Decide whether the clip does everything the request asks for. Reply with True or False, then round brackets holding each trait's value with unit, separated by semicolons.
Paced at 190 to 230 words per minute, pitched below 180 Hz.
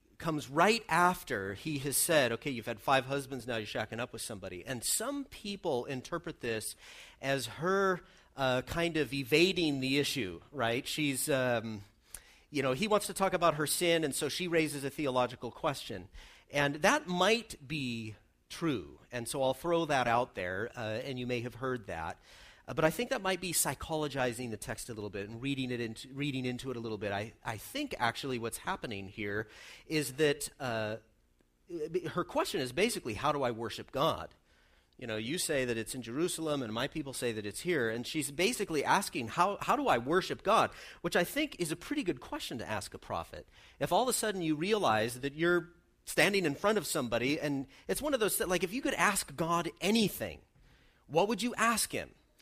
True (205 wpm; 140 Hz)